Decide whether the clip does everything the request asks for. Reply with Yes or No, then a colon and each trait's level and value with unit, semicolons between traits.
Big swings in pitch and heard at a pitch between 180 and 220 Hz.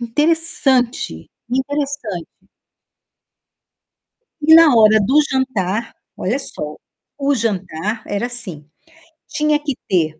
No: wide, 6.8 semitones; high, 235 Hz